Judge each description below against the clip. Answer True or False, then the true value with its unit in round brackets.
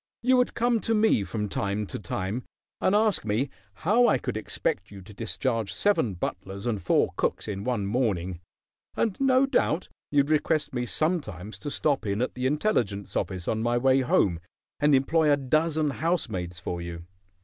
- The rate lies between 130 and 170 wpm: False (180 wpm)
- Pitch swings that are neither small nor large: False (8.0 semitones)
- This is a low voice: True (125 Hz)